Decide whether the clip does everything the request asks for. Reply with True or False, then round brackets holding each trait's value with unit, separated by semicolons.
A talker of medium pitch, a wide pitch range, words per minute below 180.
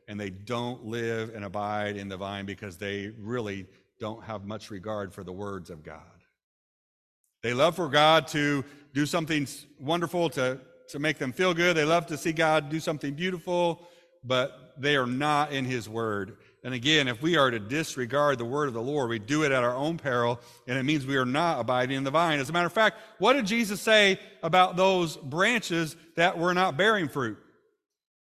False (145 Hz; 6.4 semitones; 205 wpm)